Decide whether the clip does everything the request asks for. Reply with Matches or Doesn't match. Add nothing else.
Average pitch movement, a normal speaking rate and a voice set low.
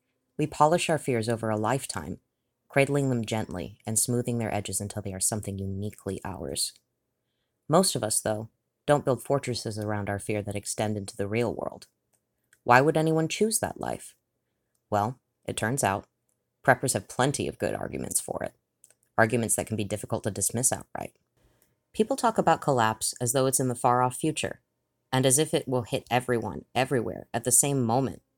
Matches